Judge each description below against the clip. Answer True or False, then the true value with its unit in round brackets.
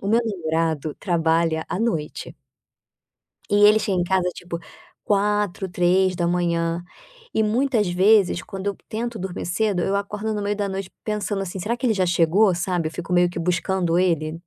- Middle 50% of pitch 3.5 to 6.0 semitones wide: False (3.1 semitones)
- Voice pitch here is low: False (185 Hz)